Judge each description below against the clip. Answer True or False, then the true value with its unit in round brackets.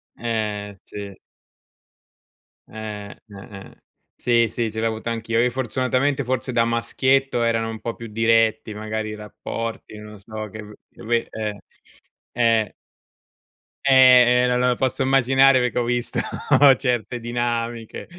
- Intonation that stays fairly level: True (2.2 semitones)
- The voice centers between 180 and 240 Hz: False (115 Hz)